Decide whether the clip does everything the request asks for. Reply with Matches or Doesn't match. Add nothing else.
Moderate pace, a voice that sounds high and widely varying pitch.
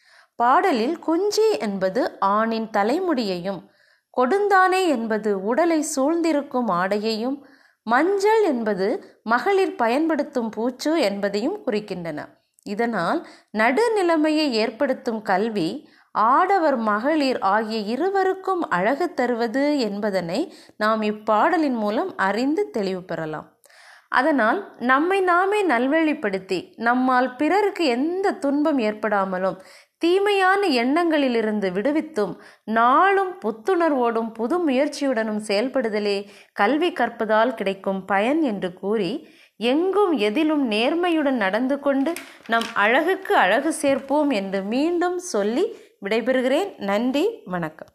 Matches